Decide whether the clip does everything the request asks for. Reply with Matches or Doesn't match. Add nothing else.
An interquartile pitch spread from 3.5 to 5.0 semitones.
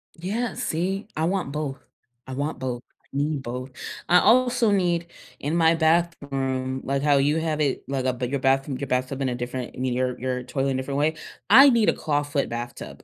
Matches